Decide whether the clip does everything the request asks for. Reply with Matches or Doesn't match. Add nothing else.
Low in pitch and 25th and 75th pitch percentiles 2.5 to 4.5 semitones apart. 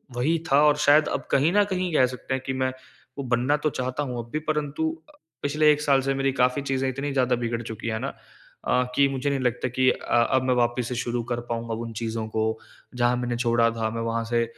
Matches